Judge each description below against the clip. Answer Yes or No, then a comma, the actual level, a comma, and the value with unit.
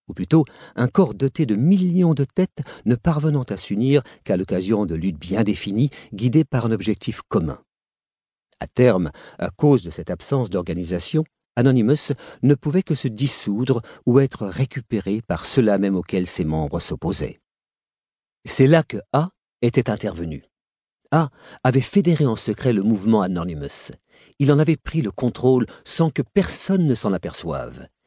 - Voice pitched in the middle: No, low, 125 Hz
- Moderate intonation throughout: No, wide, 6.4 semitones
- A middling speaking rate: Yes, average, 160 wpm